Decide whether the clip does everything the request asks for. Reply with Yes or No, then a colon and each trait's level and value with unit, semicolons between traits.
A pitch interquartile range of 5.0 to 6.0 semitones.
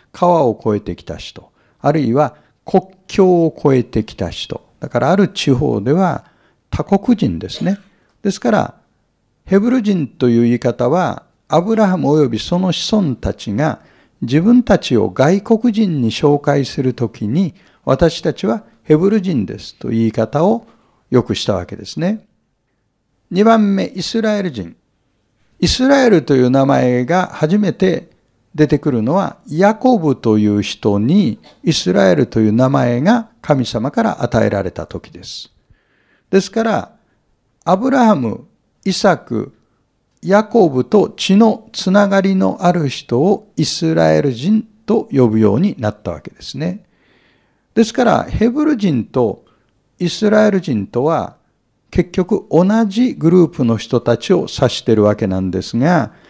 No: wide, 8.9 semitones